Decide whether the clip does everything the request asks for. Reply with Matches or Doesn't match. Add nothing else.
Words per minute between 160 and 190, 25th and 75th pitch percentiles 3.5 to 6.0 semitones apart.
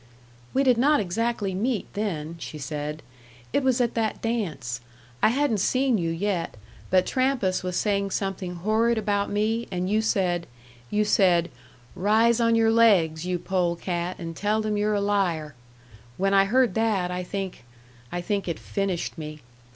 Matches